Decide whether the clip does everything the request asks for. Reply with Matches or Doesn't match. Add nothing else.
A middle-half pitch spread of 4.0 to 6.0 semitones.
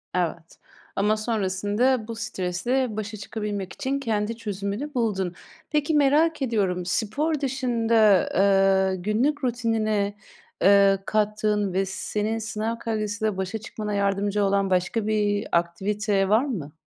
Doesn't match